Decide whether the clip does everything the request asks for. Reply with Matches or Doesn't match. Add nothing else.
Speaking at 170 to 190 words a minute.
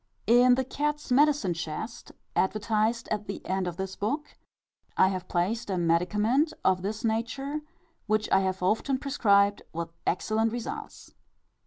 Doesn't match